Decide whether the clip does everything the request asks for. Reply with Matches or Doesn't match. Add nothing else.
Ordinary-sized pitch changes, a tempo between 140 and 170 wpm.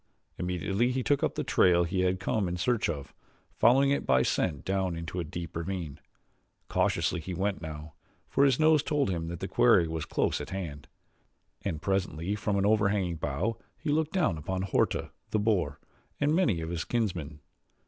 Doesn't match